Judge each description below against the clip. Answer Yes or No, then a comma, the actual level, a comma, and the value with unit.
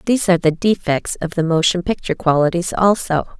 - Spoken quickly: No, average, 175 wpm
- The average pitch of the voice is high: No, medium, 175 Hz